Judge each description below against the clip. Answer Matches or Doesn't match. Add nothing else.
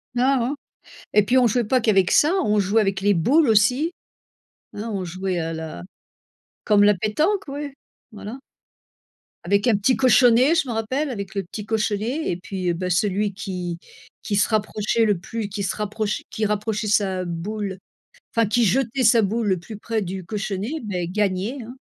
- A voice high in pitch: Matches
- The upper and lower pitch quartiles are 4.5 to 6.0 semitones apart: Doesn't match